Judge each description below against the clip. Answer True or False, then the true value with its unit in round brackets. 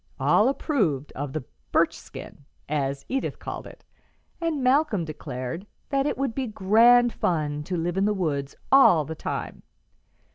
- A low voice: False (190 Hz)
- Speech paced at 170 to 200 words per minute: False (150 wpm)